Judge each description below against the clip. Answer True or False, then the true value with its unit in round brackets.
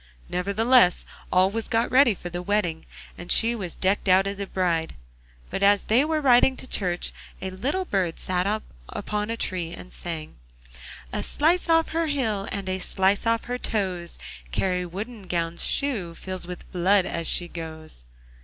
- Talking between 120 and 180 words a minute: True (170 wpm)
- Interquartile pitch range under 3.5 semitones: False (4.3 semitones)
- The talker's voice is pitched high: True (195 Hz)